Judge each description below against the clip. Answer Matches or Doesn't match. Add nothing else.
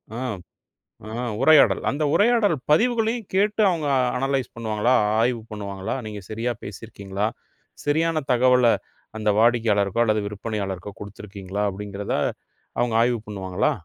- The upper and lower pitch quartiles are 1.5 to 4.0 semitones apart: Doesn't match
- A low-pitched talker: Matches